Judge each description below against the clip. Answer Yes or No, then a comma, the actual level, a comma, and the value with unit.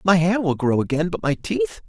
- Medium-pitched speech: Yes, medium, 160 Hz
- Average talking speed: No, fast, 255 wpm